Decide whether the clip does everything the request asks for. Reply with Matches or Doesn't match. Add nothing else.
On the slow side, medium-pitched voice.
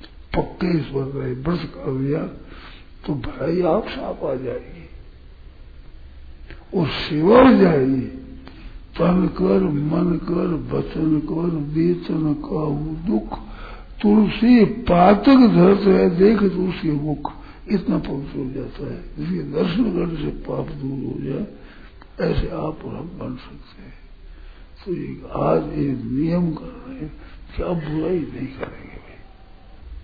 Matches